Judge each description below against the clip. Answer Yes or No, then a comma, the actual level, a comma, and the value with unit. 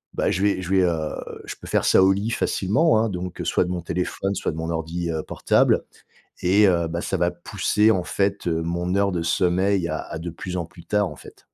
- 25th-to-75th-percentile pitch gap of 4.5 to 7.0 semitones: No, narrow, 2.6 semitones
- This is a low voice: Yes, very low, 90 Hz